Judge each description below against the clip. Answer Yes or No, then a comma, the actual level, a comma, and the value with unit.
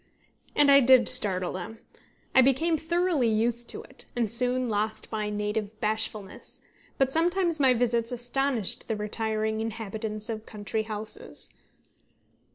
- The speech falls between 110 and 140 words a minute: Yes, slow, 135 wpm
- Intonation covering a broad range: No, average, 3.4 semitones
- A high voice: Yes, high, 225 Hz